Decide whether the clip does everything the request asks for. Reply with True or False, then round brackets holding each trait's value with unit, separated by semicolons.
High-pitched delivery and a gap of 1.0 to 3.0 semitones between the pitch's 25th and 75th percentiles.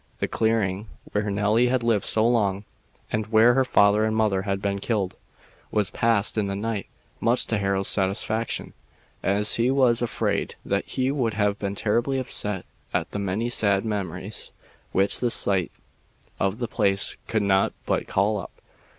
False (105 Hz; 2.6 semitones)